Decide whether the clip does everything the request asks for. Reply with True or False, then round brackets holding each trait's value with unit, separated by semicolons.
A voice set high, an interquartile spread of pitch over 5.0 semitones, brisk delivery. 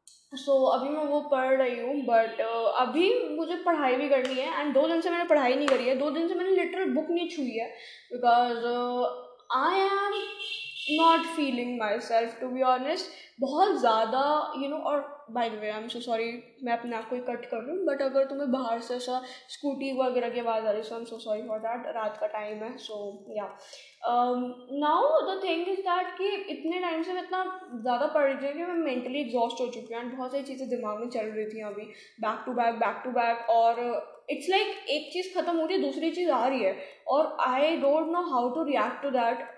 True (265 Hz; 5.4 semitones; 220 wpm)